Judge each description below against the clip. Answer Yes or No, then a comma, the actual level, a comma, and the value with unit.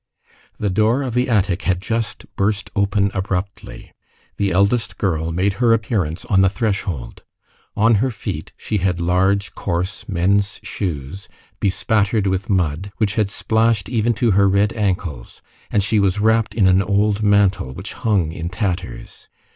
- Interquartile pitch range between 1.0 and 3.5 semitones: Yes, narrow, 2.6 semitones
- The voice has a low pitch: Yes, low, 100 Hz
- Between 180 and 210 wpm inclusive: No, average, 155 wpm